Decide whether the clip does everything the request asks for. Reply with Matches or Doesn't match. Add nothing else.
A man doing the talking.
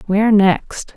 Doesn't match